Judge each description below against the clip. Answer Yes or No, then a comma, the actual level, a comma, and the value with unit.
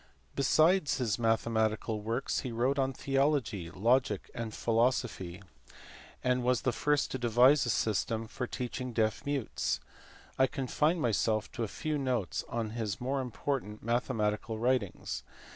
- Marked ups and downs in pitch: No, average, 3.2 semitones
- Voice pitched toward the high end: No, low, 120 Hz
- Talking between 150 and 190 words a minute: No, average, 140 wpm